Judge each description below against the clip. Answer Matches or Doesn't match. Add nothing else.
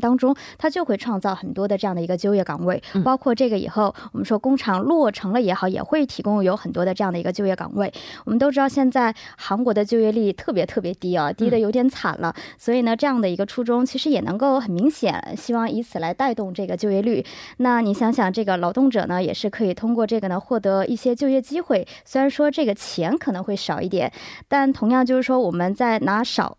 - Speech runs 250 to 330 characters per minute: Doesn't match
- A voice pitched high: Matches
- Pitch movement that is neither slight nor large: Matches